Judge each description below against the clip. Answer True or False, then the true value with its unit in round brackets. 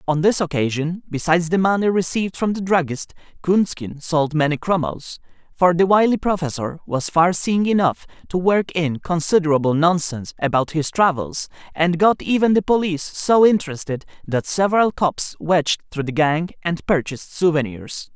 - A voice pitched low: False (170 Hz)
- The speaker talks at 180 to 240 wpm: False (155 wpm)